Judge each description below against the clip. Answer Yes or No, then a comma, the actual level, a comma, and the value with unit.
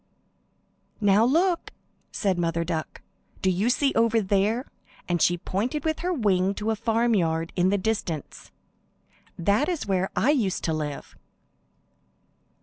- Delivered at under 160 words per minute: Yes, average, 140 wpm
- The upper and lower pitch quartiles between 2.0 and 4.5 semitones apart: No, average, 4.9 semitones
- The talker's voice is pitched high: Yes, high, 200 Hz